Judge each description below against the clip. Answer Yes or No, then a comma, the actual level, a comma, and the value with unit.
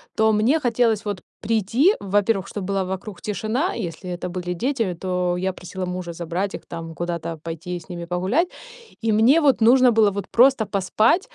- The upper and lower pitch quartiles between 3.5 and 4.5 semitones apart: Yes, average, 4.2 semitones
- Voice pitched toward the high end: Yes, high, 200 Hz